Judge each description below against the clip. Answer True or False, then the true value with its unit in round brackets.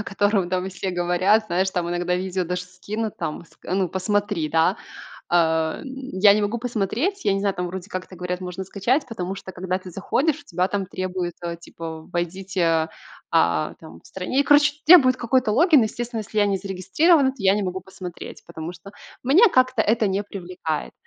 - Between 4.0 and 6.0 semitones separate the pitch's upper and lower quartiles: False (3.3 semitones)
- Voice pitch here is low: False (190 Hz)